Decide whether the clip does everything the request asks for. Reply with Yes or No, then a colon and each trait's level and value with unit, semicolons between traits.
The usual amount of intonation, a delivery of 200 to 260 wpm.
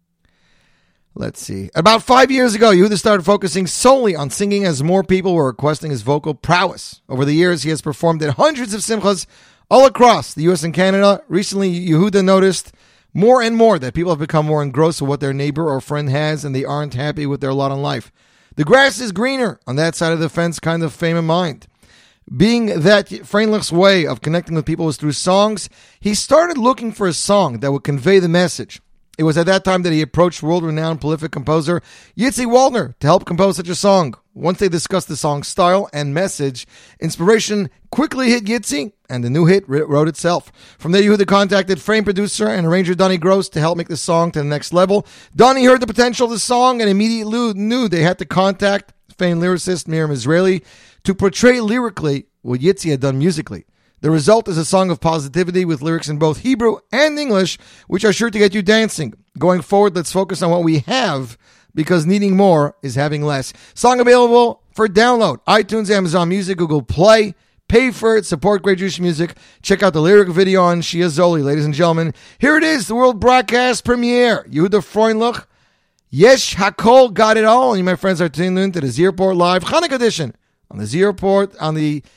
Yes: average, 4.9 semitones; fast, 205 wpm